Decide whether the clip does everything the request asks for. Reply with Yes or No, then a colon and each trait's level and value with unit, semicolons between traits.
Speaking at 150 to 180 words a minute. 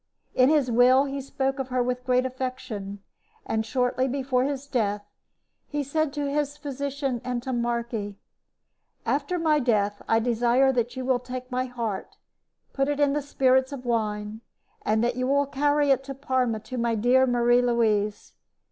Yes: average, 165 wpm